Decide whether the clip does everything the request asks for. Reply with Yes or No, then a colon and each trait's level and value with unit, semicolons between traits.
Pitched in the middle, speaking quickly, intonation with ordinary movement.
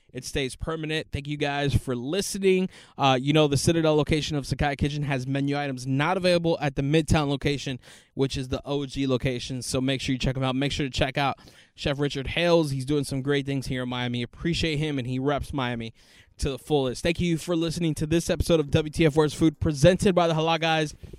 Yes: medium, 145 Hz; fast, 225 wpm; average, 3.1 semitones